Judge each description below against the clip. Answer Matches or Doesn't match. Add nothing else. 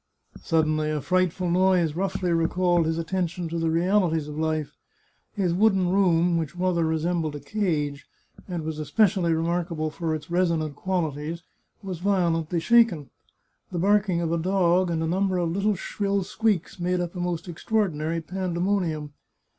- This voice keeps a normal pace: Matches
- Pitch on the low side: Doesn't match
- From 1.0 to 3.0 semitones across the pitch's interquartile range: Matches